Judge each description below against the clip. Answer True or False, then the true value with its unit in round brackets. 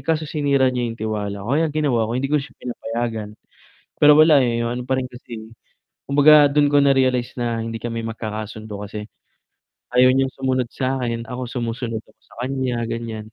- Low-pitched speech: True (125 Hz)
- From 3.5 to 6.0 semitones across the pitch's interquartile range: False (2.9 semitones)